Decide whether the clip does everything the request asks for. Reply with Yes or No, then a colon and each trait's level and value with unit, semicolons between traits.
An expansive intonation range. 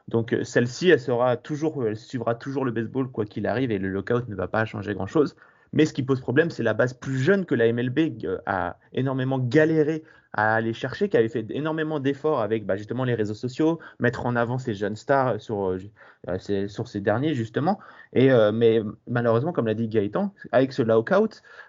No: average, 4.2 semitones